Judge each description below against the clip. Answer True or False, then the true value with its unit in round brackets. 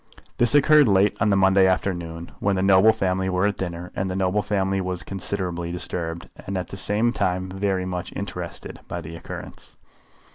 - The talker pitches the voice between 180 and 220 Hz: False (95 Hz)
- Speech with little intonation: True (1.8 semitones)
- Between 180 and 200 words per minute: True (185 wpm)